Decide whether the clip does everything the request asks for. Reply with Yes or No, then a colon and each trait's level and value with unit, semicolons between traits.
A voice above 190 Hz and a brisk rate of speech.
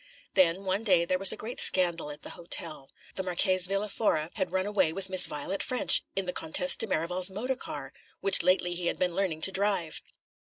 No: medium, 185 Hz; fast, 215 wpm